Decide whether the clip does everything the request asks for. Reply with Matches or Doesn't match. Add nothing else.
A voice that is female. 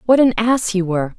Matches